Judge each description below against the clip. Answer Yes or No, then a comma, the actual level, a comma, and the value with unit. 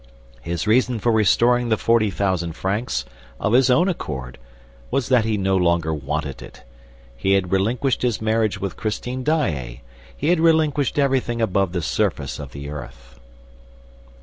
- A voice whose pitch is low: Yes, low, 105 Hz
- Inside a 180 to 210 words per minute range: No, average, 155 wpm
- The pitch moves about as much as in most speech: No, wide, 6.9 semitones